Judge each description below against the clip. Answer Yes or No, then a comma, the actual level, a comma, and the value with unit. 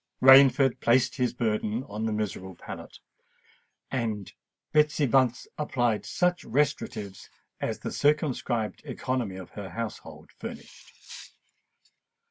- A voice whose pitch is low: Yes, low, 120 Hz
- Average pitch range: Yes, average, 4.0 semitones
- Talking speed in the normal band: No, slow, 105 wpm